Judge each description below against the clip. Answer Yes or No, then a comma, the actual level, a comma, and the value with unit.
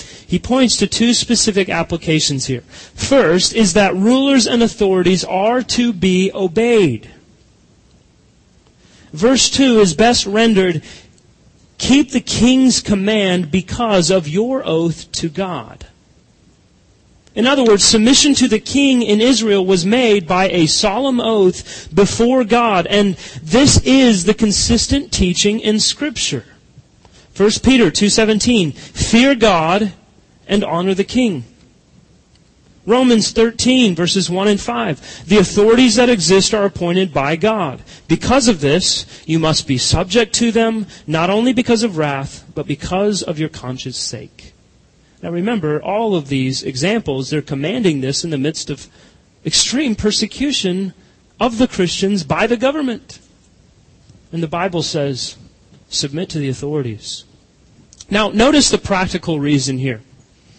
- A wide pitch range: Yes, wide, 6.2 semitones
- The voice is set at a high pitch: Yes, high, 195 Hz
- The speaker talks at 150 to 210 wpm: No, slow, 135 wpm